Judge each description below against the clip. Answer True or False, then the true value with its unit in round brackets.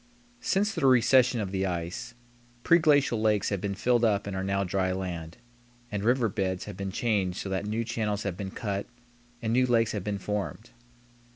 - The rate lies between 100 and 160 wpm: False (190 wpm)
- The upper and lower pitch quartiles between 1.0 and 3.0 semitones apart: False (3.6 semitones)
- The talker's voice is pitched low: True (105 Hz)